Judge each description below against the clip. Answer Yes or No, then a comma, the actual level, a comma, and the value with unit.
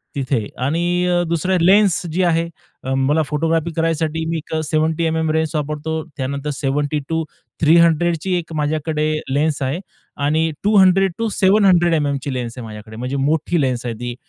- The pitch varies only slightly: No, average, 3.1 semitones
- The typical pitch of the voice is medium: Yes, medium, 160 Hz